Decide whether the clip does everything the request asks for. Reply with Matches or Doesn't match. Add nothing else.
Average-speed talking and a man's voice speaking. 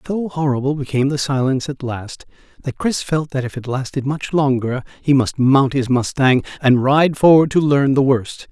Matches